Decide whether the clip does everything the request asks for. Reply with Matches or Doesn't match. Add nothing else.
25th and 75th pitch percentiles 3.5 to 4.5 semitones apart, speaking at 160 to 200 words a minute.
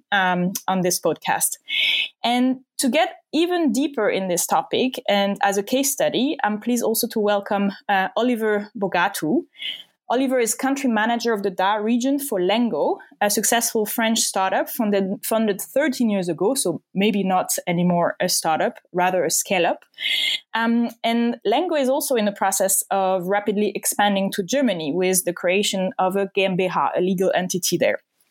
Doesn't match